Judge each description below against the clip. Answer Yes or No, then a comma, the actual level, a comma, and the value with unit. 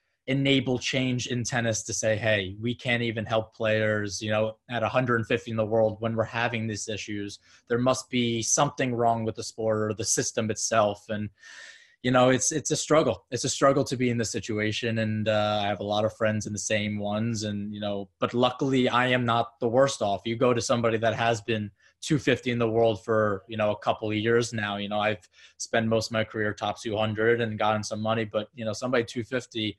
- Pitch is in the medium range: No, low, 115 Hz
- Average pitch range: No, narrow, 2.0 semitones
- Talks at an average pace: No, fast, 225 wpm